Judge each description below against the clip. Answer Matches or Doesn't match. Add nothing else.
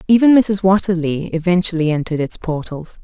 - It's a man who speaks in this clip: Doesn't match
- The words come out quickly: Doesn't match